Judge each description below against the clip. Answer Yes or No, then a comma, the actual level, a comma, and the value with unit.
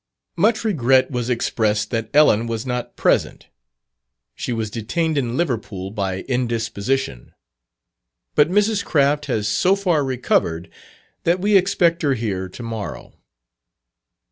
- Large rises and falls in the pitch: Yes, wide, 6.6 semitones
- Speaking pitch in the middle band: No, low, 125 Hz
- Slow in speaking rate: Yes, slow, 125 wpm